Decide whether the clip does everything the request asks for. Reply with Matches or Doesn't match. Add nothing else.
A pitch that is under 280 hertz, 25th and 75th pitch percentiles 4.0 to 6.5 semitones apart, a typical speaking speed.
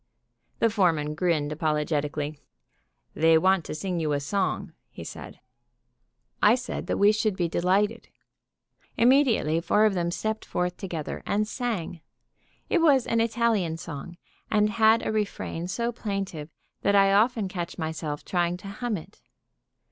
Matches